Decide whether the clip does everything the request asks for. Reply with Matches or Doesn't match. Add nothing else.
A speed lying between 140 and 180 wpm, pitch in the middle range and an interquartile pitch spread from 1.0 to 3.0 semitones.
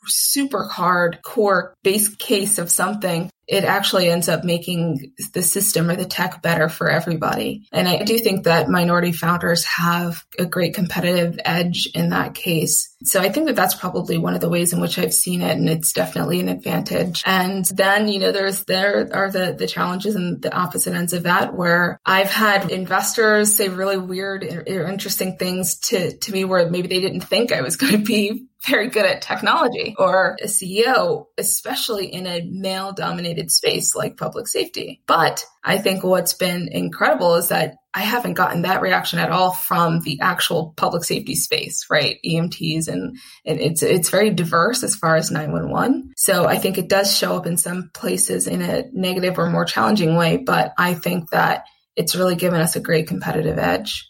Doesn't match